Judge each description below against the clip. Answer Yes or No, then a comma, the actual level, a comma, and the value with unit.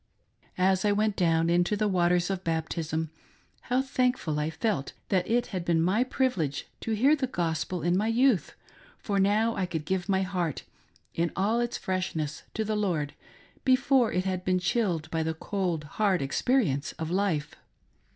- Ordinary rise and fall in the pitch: Yes, average, 4.8 semitones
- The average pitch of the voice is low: No, medium, 185 Hz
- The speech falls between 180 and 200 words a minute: No, average, 170 wpm